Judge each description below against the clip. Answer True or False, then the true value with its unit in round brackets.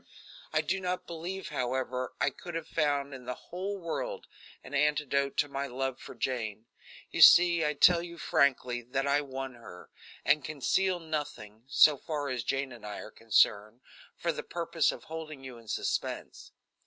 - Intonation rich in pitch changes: False (4.4 semitones)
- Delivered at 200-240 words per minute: False (175 wpm)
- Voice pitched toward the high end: False (140 Hz)